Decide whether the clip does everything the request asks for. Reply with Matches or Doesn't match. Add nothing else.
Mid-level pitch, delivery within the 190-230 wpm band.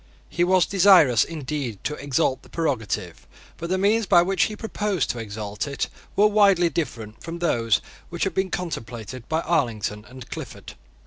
Doesn't match